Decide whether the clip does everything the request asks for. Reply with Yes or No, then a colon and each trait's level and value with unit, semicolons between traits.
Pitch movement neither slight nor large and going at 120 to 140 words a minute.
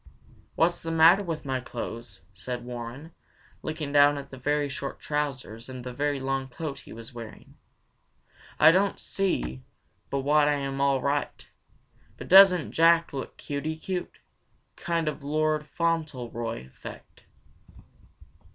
Yes: average, 3.9 semitones; slow, 135 wpm